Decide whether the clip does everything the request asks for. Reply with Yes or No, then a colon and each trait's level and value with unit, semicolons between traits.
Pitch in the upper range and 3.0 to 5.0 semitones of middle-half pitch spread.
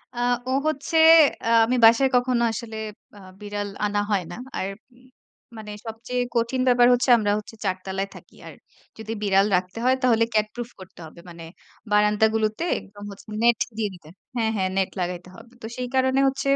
Yes: high, 220 Hz; average, 3.5 semitones